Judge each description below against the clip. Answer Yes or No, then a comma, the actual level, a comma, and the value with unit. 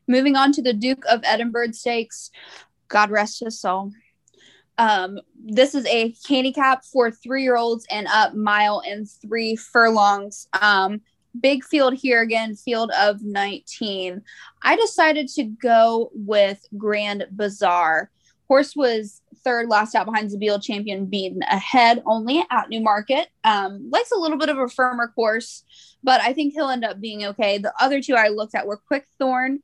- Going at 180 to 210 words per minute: No, average, 160 wpm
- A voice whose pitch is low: No, high, 230 Hz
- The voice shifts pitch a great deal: No, average, 3.8 semitones